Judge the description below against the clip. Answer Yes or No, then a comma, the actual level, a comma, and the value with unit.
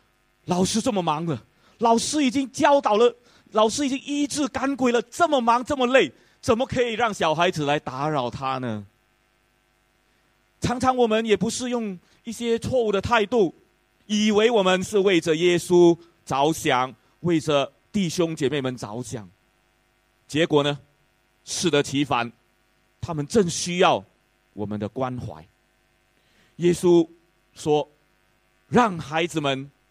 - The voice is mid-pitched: Yes, medium, 170 Hz